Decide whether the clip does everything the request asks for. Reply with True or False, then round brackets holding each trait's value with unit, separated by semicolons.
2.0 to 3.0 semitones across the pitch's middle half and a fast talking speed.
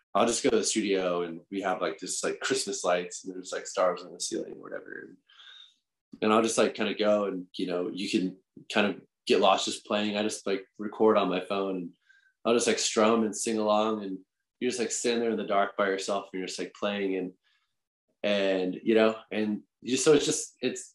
True (2.7 semitones; 240 wpm)